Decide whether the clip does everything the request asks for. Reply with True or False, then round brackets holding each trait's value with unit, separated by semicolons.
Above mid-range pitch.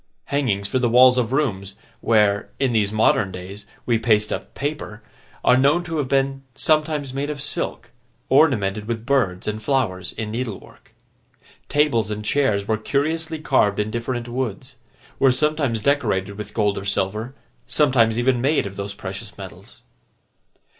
False (120 Hz)